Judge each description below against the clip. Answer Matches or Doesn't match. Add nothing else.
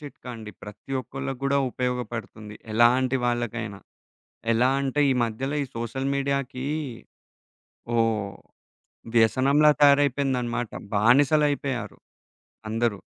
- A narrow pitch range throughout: Doesn't match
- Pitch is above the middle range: Doesn't match